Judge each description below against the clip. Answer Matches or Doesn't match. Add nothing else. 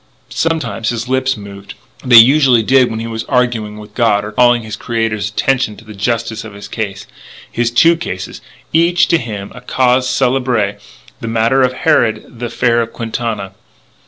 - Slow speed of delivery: Doesn't match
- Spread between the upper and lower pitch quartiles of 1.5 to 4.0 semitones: Matches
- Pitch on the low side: Matches